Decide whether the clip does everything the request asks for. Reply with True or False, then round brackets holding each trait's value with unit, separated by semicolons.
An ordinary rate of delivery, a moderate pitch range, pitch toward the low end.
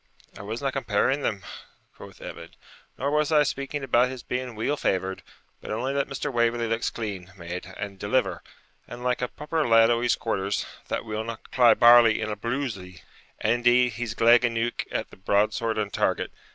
True (185 wpm; 3.1 semitones; 115 Hz)